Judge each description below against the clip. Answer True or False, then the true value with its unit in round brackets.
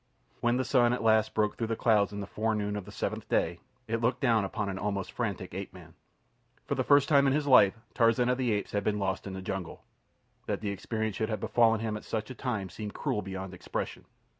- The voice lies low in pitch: True (110 Hz)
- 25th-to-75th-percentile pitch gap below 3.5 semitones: True (2.9 semitones)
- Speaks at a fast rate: True (240 wpm)